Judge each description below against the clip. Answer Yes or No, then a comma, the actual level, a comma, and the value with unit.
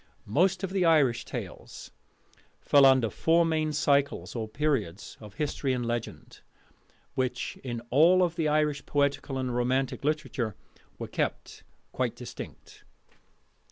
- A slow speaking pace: Yes, slow, 125 wpm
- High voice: No, medium, 140 Hz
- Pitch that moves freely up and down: No, average, 3.9 semitones